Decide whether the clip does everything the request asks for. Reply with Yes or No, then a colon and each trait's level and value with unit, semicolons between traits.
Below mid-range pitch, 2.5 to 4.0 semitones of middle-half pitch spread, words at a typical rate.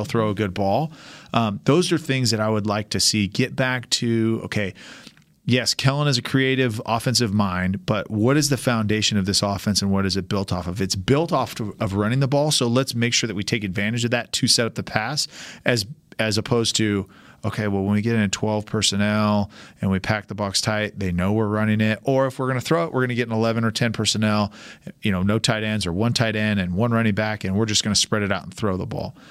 No: low, 110 Hz; average, 2.9 semitones; fast, 260 wpm